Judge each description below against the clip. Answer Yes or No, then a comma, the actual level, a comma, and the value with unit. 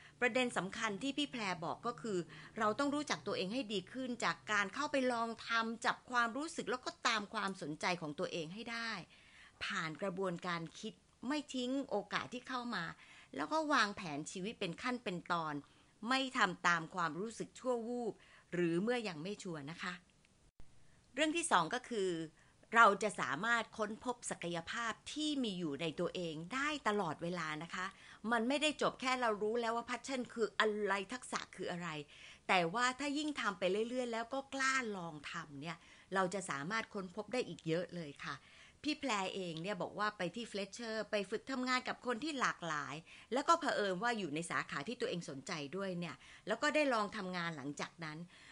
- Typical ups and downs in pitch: No, wide, 5.9 semitones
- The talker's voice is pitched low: No, high, 210 Hz